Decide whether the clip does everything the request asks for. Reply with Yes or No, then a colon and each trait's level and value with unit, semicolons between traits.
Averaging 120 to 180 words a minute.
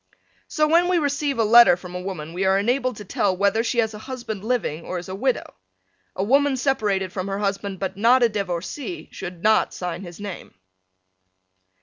No: average, 200 wpm